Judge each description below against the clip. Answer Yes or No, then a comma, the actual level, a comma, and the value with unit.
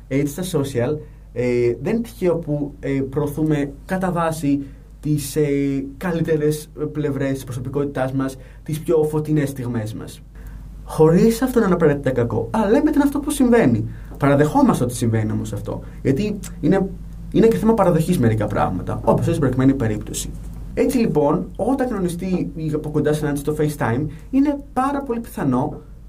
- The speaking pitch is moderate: Yes, medium, 150 Hz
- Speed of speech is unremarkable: Yes, average, 155 wpm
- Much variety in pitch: No, average, 4.5 semitones